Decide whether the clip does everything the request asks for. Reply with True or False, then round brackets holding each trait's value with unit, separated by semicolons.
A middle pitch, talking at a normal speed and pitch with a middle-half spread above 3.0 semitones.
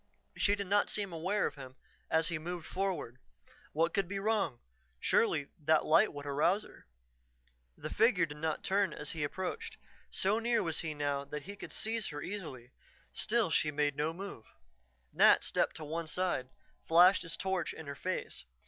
True (165 Hz; 180 wpm; 4.9 semitones)